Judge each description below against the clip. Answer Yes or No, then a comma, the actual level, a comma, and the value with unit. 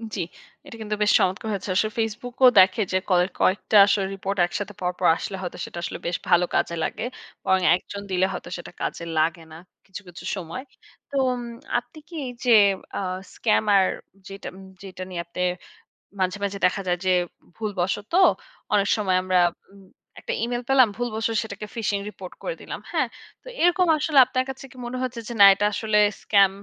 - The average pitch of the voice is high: Yes, high, 200 Hz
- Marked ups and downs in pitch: No, average, 3.4 semitones